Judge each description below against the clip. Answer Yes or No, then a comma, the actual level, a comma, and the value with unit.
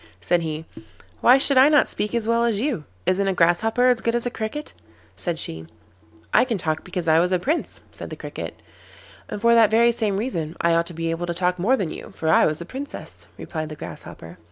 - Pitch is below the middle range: No, high, 195 Hz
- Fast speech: Yes, fast, 230 wpm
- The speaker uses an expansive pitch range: Yes, wide, 5.9 semitones